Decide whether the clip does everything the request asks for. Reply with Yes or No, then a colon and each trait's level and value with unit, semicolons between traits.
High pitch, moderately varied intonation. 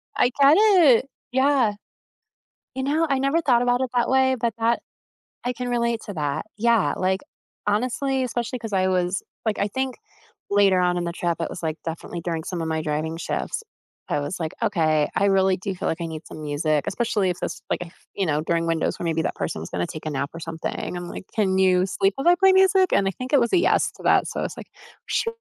No: high, 195 Hz; wide, 7.2 semitones